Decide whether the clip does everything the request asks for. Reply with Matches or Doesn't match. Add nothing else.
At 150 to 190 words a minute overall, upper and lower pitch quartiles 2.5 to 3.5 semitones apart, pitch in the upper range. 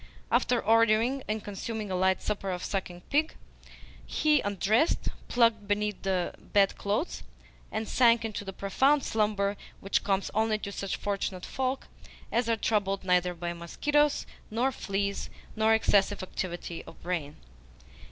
Doesn't match